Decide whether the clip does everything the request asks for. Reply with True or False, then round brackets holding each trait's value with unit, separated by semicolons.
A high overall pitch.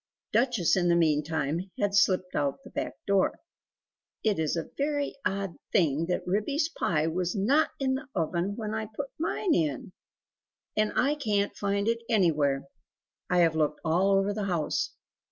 True (195 Hz)